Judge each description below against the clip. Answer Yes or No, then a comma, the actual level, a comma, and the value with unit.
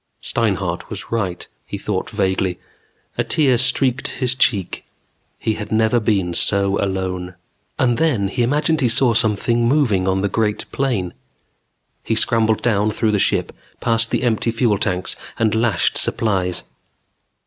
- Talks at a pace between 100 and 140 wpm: No, average, 155 wpm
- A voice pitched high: No, low, 110 Hz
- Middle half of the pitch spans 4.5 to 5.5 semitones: No, average, 3.7 semitones